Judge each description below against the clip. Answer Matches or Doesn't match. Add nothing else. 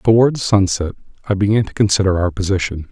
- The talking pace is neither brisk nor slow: Matches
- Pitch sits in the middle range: Doesn't match